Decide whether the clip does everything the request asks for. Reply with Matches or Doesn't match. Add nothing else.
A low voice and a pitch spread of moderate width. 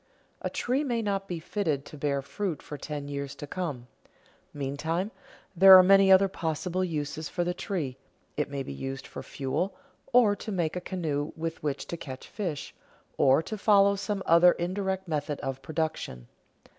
Doesn't match